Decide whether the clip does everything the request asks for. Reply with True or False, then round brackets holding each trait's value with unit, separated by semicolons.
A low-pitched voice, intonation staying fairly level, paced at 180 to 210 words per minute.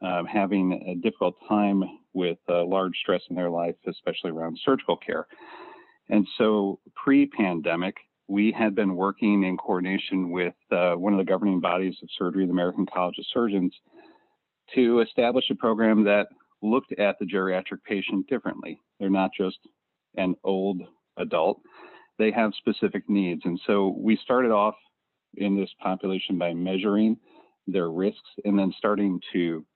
False (95 Hz; 2.1 semitones; 155 wpm)